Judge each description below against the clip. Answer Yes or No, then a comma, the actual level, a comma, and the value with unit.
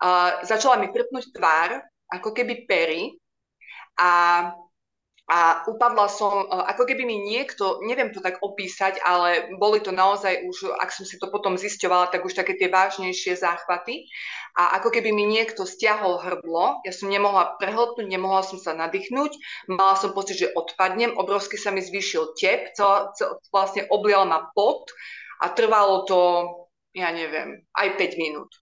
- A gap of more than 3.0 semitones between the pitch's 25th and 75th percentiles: No, narrow, 2.5 semitones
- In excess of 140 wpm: Yes, average, 160 wpm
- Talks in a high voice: Yes, high, 195 Hz